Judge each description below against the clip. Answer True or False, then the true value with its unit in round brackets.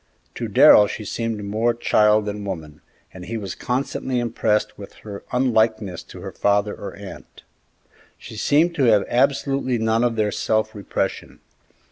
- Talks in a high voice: False (110 Hz)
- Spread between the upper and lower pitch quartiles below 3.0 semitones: True (2.6 semitones)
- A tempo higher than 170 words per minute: False (155 wpm)